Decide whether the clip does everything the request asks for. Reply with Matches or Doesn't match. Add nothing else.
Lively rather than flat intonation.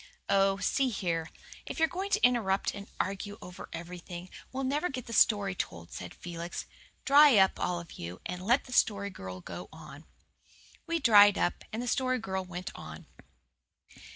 Matches